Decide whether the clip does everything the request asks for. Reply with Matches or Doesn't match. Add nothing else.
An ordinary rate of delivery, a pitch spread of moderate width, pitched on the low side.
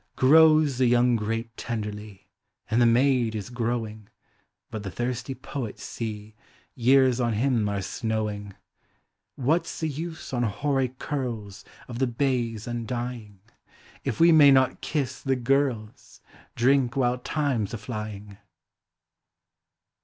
Doesn't match